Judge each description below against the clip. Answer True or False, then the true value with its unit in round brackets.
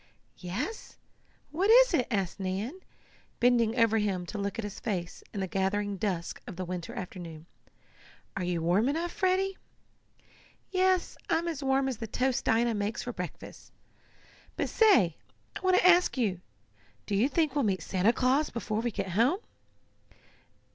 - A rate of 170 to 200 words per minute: False (160 wpm)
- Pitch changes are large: True (7.6 semitones)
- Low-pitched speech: False (225 Hz)